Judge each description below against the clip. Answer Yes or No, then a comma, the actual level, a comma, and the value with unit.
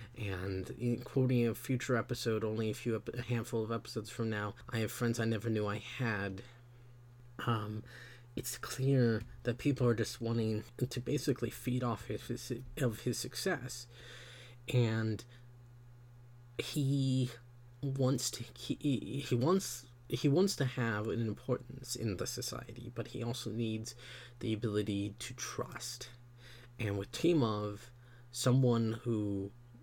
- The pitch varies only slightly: Yes, narrow, 1.6 semitones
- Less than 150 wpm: Yes, average, 140 wpm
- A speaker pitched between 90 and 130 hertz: Yes, low, 120 Hz